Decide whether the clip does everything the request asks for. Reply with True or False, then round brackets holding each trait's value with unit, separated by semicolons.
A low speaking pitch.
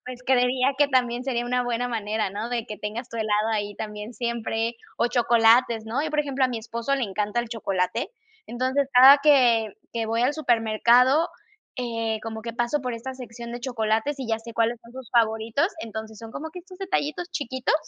False (235 Hz)